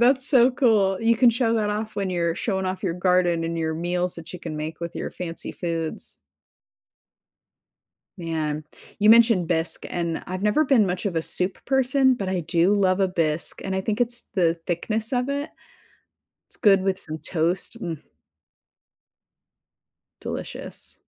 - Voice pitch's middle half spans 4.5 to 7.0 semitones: Yes, average, 4.9 semitones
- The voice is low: No, medium, 185 Hz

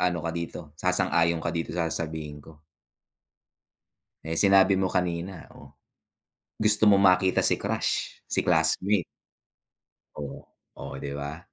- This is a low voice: Yes, very low, 85 Hz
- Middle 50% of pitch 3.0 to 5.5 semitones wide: No, narrow, 2.6 semitones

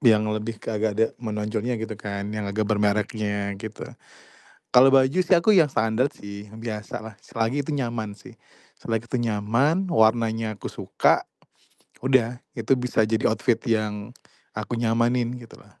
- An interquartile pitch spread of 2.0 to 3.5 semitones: Yes, narrow, 2.4 semitones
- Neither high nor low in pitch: No, low, 110 Hz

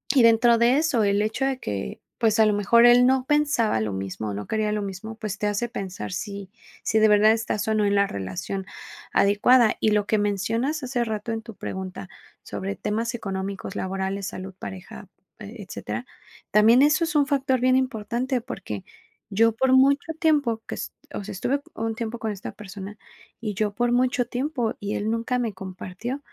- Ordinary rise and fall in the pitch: Yes, average, 3.6 semitones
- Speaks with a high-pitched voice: Yes, high, 220 Hz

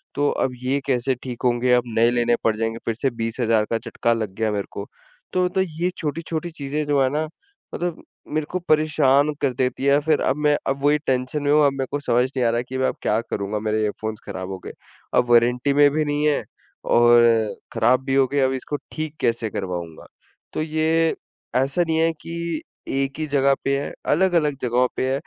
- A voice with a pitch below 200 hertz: Yes, low, 135 Hz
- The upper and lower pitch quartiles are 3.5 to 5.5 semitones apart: Yes, average, 4.2 semitones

